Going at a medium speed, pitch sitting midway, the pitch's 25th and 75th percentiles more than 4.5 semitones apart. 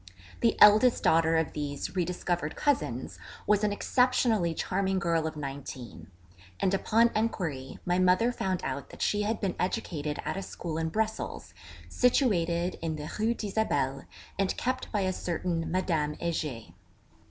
Yes: average, 155 wpm; medium, 180 Hz; average, 4.9 semitones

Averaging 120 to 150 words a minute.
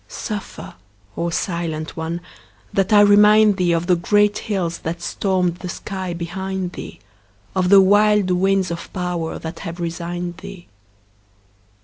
Yes: average, 140 wpm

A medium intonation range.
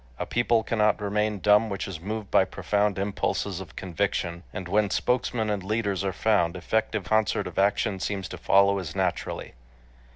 No: narrow, 2.0 semitones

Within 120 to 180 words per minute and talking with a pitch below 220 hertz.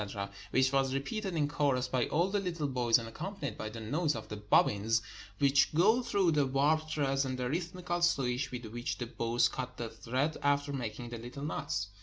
No: fast, 205 wpm; low, 135 Hz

